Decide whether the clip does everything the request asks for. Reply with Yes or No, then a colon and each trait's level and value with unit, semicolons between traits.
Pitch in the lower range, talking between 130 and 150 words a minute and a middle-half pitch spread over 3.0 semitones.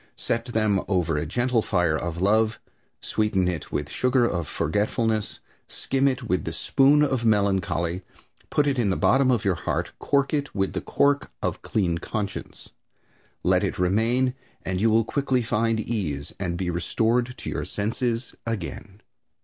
No: low, 110 Hz; average, 165 wpm; average, 4.9 semitones